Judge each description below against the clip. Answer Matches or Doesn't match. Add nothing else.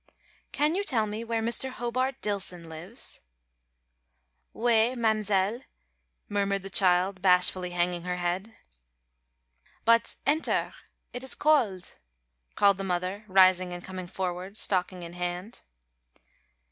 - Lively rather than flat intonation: Doesn't match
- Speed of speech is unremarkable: Doesn't match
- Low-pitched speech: Doesn't match